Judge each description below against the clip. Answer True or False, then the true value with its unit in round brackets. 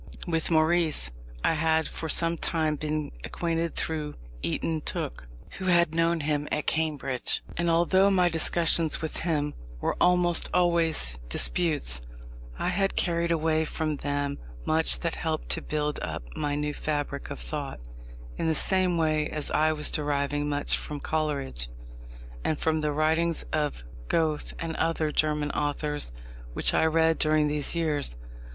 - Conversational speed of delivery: True (150 wpm)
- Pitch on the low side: False (155 Hz)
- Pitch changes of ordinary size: False (2.0 semitones)